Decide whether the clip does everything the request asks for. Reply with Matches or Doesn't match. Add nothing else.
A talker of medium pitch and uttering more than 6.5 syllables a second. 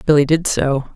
Doesn't match